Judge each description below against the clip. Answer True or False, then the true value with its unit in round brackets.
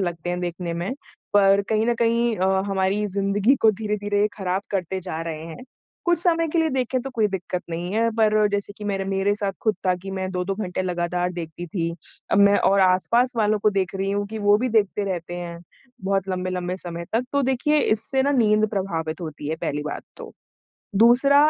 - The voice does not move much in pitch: False (3.3 semitones)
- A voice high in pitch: True (195 Hz)